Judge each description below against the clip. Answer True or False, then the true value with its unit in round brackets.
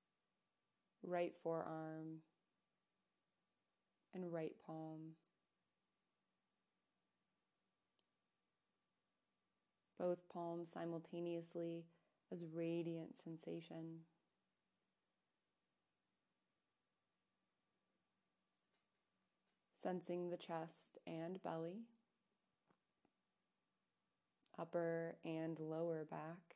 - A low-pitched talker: False (165 Hz)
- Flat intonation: True (1.0 semitones)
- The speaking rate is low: True (45 wpm)